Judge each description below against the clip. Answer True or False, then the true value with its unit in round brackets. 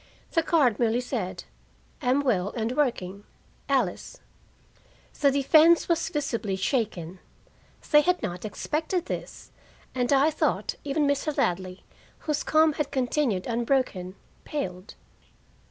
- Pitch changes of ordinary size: False (6.7 semitones)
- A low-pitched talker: False (255 Hz)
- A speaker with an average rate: False (120 wpm)